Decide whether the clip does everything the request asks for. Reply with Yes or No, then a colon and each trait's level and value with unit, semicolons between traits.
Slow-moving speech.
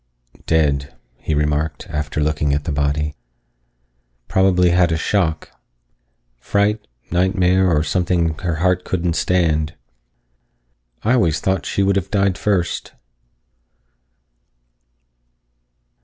Yes: slow, 105 wpm